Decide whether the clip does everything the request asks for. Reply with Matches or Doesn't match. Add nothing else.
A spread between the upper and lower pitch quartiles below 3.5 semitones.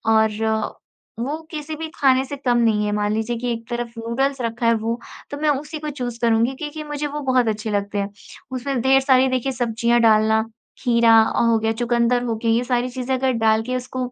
Matches